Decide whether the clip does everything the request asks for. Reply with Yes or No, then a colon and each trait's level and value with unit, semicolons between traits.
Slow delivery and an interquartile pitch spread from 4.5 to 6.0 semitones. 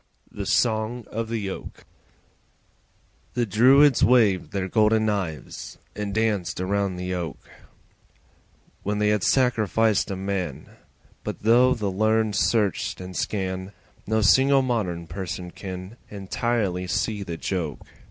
No: slow, 125 wpm; average, 3.3 semitones